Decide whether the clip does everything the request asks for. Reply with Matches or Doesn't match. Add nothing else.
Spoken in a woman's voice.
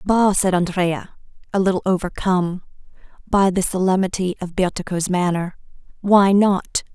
Matches